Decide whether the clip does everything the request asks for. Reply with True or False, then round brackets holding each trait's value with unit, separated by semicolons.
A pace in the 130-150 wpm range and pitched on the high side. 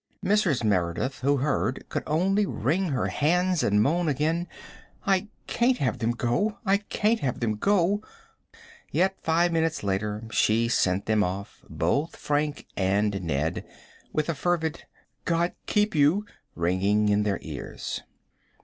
False (140 wpm; 145 Hz)